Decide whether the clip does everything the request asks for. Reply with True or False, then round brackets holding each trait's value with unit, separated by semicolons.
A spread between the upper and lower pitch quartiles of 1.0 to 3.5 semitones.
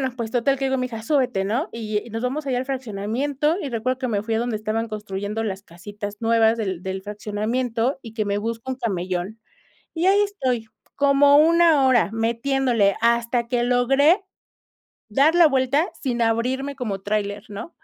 False (3.9 semitones)